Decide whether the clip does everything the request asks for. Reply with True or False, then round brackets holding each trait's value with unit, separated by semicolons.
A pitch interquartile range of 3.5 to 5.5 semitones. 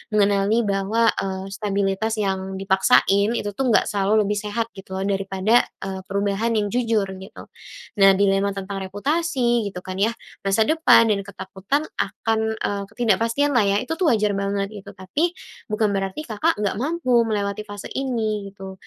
False (2.7 semitones)